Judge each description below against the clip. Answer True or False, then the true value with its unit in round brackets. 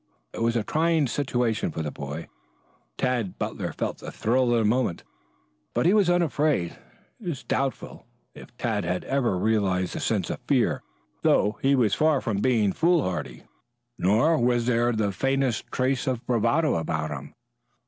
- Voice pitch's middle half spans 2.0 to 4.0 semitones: False (5.4 semitones)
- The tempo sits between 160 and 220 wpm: True (165 wpm)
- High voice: False (120 Hz)